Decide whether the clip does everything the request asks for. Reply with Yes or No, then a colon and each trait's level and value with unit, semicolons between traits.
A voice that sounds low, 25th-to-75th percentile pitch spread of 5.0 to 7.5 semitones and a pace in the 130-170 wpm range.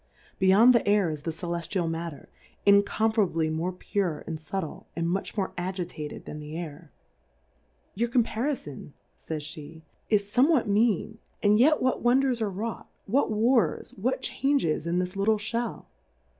No: high, 195 Hz; wide, 5.4 semitones; average, 150 wpm